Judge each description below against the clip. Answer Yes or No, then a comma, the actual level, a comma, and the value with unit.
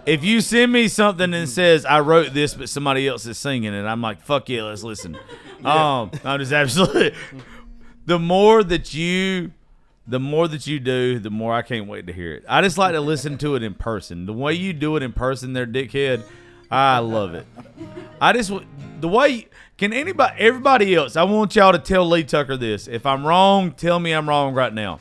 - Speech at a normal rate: No, fast, 215 wpm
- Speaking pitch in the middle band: Yes, medium, 145 Hz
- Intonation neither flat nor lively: No, wide, 6.1 semitones